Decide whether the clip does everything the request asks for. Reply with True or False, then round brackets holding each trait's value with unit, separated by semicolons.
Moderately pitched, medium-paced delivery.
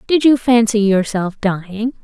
False (220 Hz; 145 wpm)